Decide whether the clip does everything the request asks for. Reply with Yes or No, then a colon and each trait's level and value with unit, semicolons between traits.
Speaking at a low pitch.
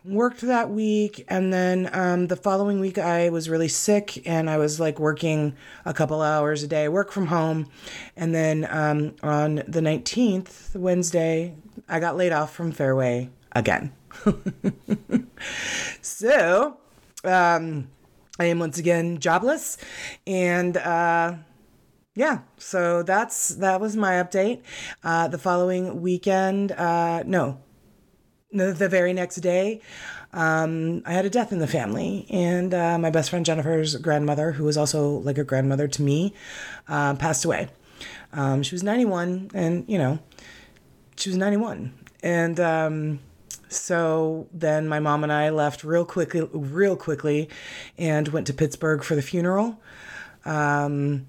No: medium, 170 Hz